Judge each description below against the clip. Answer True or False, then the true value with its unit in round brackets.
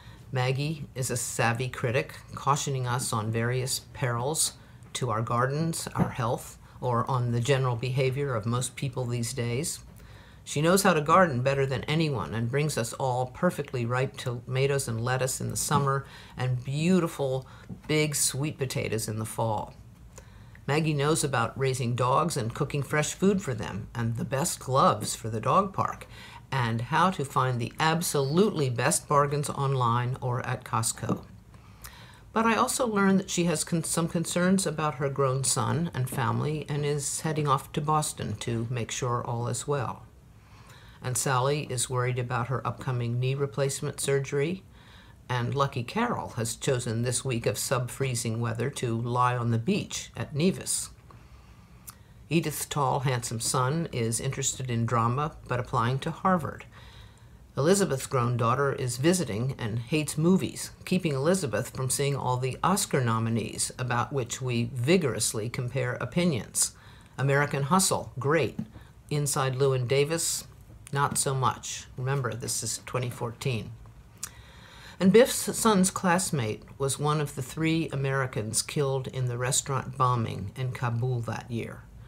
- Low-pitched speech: True (130 Hz)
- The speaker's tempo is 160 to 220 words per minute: False (150 wpm)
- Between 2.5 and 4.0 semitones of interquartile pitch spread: True (3.5 semitones)